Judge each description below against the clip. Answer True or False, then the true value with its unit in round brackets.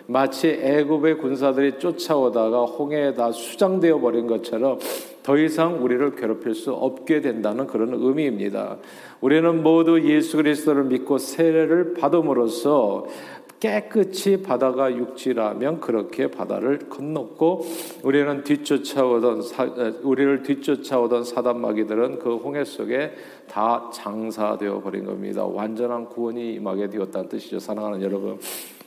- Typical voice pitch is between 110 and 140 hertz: True (135 Hz)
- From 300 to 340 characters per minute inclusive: True (310 characters per minute)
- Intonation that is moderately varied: True (4.9 semitones)